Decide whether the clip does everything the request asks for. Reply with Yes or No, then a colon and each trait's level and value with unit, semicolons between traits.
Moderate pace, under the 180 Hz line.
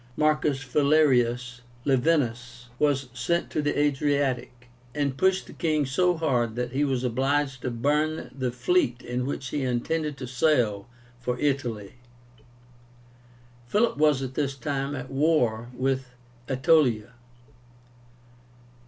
No: slow, 125 wpm; low, 135 Hz